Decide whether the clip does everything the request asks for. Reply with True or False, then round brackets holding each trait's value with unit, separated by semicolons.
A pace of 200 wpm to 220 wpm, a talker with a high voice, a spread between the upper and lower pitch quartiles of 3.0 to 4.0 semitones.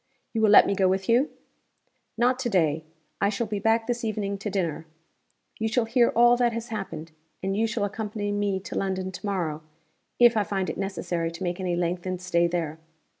True (205 wpm; 200 Hz; 3.7 semitones)